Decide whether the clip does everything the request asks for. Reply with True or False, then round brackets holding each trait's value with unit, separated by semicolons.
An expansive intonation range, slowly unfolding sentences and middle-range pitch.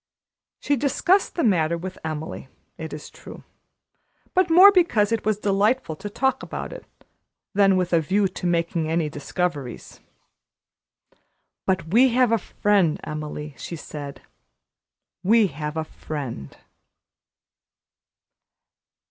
True (6.3 semitones; 125 wpm; 180 Hz)